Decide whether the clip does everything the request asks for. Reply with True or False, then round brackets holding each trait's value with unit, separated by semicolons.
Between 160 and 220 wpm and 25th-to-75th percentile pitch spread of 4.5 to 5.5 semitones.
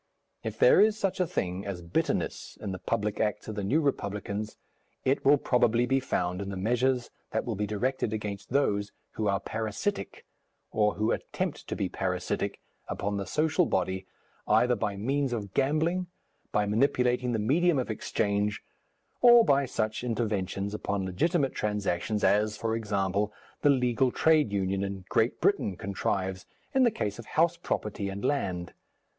True (165 wpm; 5.0 semitones)